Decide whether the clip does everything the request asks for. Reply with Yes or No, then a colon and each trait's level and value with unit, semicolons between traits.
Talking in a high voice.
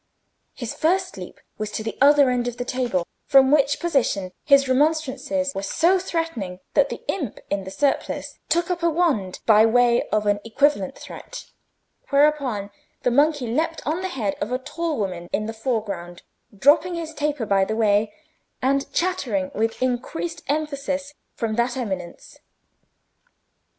Yes: very high, 260 Hz